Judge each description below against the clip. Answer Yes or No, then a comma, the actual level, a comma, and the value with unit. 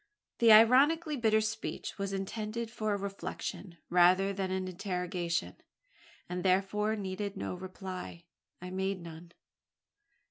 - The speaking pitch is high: Yes, high, 195 Hz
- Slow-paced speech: Yes, slow, 120 wpm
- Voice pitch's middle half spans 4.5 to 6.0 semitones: No, average, 2.9 semitones